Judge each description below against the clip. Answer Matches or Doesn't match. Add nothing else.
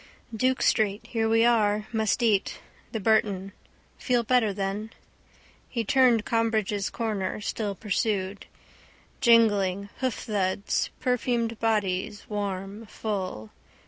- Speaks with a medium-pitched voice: Doesn't match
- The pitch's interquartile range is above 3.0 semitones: Doesn't match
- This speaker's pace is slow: Matches